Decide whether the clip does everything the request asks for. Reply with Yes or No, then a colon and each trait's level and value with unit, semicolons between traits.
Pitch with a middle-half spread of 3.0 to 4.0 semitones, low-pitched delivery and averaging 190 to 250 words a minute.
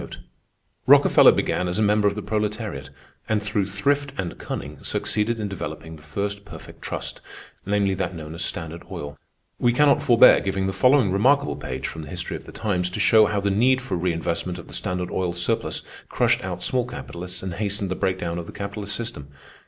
Yes: average, 3.3 semitones; low, 100 Hz; average, 195 wpm